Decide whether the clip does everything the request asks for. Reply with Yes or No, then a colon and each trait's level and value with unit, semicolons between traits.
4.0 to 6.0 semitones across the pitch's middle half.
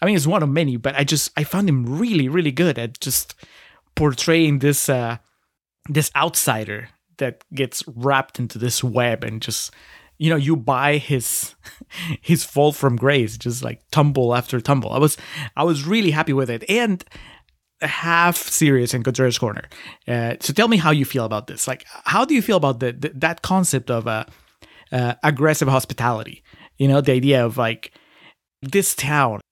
Yes: average, 4.3 semitones